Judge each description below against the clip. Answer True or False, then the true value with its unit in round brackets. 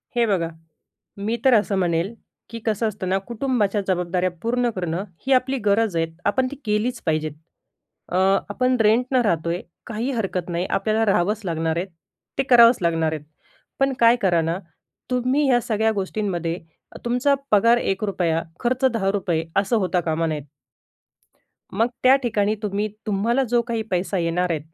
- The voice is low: False (205 Hz)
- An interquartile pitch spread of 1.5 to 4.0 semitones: False (5.0 semitones)